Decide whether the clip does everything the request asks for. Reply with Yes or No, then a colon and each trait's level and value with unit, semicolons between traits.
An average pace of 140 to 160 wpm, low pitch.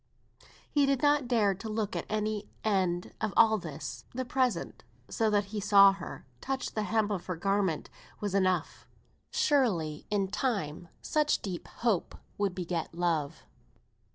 No: average, 155 wpm; high, 200 Hz